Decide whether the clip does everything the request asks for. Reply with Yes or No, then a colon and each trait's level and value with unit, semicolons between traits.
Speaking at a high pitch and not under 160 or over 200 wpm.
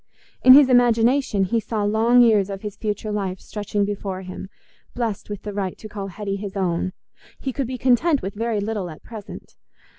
Yes: high, 210 Hz; average, 190 wpm